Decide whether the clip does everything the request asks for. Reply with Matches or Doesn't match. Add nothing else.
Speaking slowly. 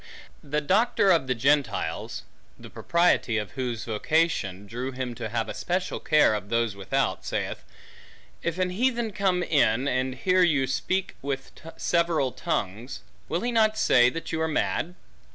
Doesn't match